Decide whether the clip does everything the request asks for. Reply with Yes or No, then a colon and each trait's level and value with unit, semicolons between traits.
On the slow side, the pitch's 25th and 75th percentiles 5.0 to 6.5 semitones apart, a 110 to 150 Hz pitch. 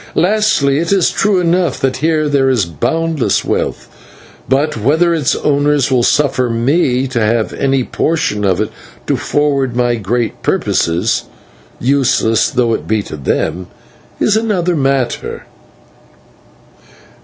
Yes: slow, 130 wpm; average, 5.3 semitones; low, 135 Hz